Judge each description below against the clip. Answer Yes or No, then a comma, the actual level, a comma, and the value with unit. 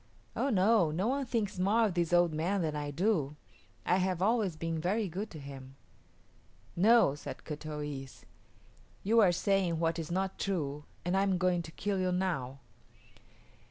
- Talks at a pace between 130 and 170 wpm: No, average, 180 wpm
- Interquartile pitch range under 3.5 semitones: No, average, 4.2 semitones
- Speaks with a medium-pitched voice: Yes, medium, 180 Hz